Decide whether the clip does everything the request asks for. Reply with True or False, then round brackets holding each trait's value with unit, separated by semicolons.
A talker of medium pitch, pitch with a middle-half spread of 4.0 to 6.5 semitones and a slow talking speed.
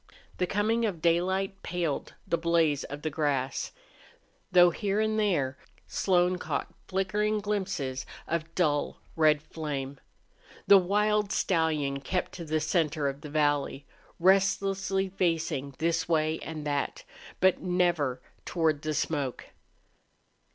True (165 Hz; 4.4 semitones; 125 wpm)